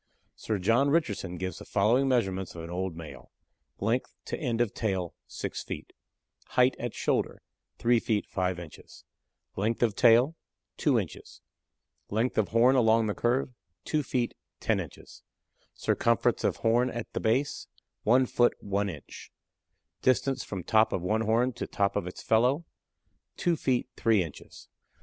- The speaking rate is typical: Yes, average, 155 wpm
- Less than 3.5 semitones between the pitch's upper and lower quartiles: No, average, 4.4 semitones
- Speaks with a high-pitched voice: No, low, 115 Hz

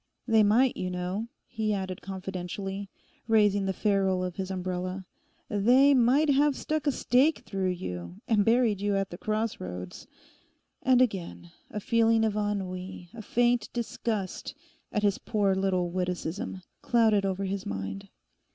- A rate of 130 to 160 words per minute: Yes, average, 145 wpm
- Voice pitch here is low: No, high, 200 Hz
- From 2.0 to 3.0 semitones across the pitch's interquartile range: No, average, 3.5 semitones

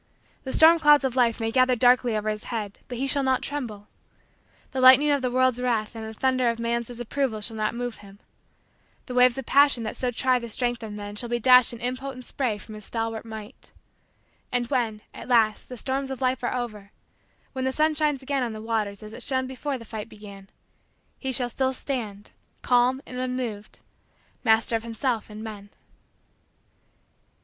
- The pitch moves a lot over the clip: No, average, 2.9 semitones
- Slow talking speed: No, average, 195 wpm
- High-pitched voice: Yes, high, 245 Hz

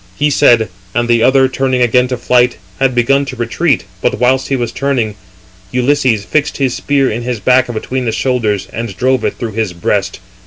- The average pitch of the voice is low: Yes, low, 125 Hz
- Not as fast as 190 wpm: No, average, 200 wpm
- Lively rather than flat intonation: No, narrow, 2.4 semitones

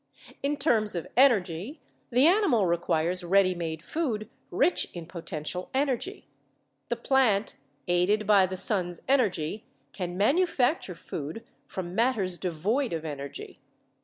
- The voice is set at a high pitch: Yes, high, 195 Hz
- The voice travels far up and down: Yes, wide, 6.4 semitones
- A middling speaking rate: No, slow, 125 wpm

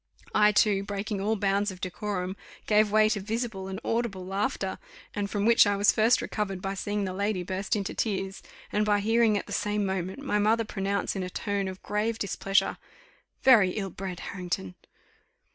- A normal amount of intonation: No, narrow, 1.8 semitones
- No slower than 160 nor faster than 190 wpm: Yes, average, 185 wpm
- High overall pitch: Yes, high, 205 Hz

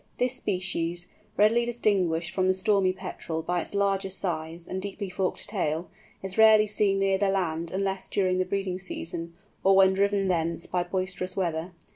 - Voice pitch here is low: No, high, 190 Hz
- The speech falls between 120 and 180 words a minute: Yes, average, 170 wpm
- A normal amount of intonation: No, narrow, 2.0 semitones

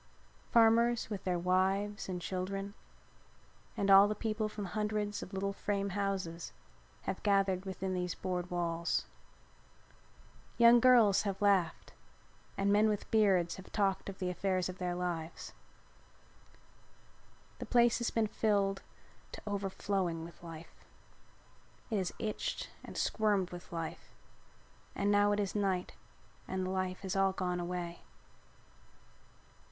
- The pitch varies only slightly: Yes, narrow, 2.3 semitones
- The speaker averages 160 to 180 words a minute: No, slow, 135 wpm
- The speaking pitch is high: Yes, high, 195 Hz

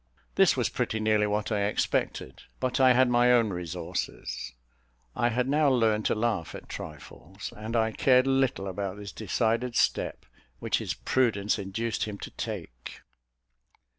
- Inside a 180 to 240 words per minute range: No, average, 155 wpm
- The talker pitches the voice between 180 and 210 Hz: No, low, 110 Hz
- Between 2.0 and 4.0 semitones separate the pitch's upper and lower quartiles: Yes, average, 3.6 semitones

